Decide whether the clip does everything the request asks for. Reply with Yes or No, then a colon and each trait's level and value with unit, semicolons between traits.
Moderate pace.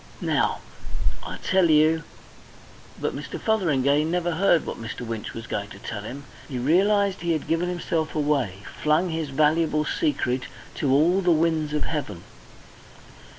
Yes: average, 155 wpm